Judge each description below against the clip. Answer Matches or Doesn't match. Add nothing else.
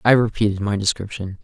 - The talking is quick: Doesn't match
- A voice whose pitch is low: Matches